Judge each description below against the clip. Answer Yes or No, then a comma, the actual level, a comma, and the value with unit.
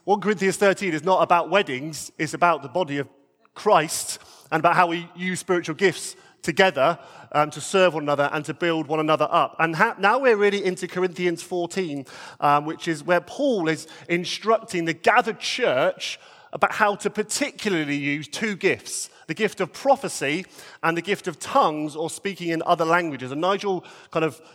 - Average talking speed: Yes, average, 185 wpm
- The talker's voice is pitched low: No, medium, 175 Hz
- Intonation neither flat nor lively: Yes, average, 3.3 semitones